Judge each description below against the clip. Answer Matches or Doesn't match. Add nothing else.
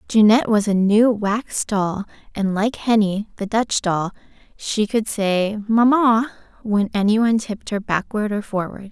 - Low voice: Doesn't match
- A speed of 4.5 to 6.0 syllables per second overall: Doesn't match